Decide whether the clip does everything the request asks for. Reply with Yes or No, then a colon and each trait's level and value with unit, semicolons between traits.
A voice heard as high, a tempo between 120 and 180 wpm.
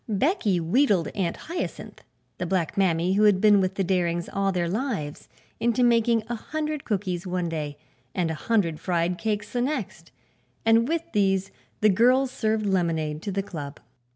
Yes: high, 195 Hz; average, 170 wpm